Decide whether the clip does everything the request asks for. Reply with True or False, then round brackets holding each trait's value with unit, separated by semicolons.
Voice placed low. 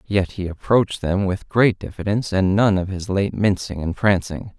True (95 Hz)